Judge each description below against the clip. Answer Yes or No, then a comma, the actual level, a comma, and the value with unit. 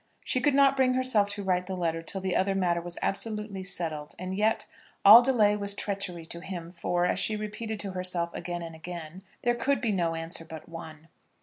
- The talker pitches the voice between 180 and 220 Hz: Yes, high, 190 Hz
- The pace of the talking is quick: Yes, fast, 210 wpm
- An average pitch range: Yes, average, 3.7 semitones